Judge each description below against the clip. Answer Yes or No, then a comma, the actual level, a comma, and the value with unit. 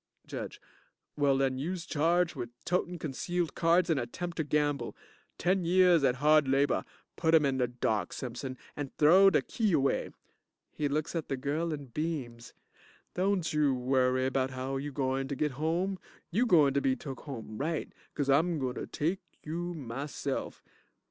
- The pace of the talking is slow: No, average, 160 wpm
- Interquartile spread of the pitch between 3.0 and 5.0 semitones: Yes, average, 4.0 semitones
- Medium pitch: Yes, medium, 145 Hz